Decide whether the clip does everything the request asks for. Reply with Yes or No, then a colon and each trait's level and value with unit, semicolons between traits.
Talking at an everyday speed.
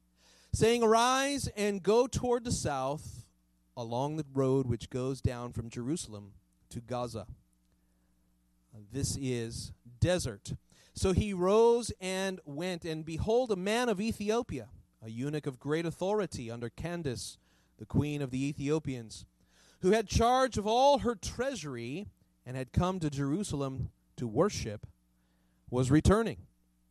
No: slow, 130 wpm